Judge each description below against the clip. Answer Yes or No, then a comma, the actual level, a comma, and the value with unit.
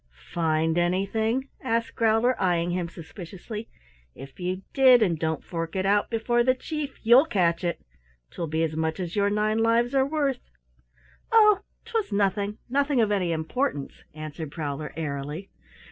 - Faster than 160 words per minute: No, average, 155 wpm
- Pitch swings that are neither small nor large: No, wide, 6.4 semitones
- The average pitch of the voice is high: Yes, high, 200 Hz